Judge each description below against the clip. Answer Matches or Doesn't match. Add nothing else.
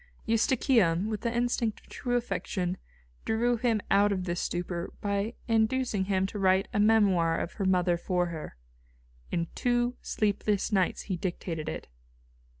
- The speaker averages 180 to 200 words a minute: Doesn't match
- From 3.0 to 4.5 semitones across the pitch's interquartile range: Matches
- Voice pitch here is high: Matches